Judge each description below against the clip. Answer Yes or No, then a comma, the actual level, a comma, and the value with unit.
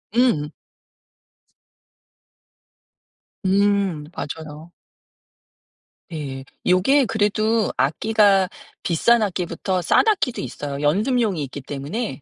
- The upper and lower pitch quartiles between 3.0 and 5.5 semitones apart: No, wide, 6.5 semitones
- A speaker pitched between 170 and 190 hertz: Yes, medium, 185 Hz